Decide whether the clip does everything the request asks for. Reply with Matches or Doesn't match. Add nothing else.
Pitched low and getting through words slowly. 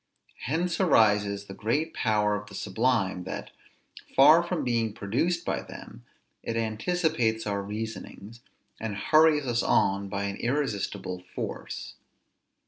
Matches